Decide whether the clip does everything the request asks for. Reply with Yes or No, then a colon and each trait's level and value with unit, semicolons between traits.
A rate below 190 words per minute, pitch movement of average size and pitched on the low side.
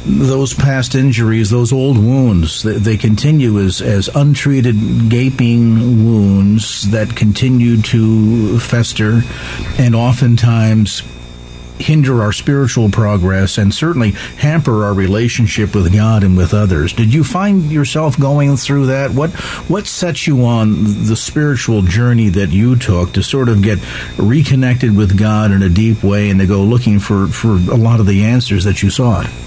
Yes: average, 155 wpm; average, 4.1 semitones; low, 115 Hz